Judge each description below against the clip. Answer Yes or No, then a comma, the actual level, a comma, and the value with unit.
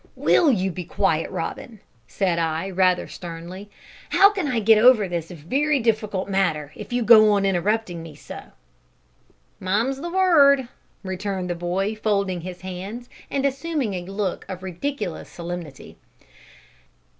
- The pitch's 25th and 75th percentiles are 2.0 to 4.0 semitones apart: No, average, 5.2 semitones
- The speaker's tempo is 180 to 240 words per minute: No, average, 145 wpm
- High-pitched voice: Yes, high, 195 Hz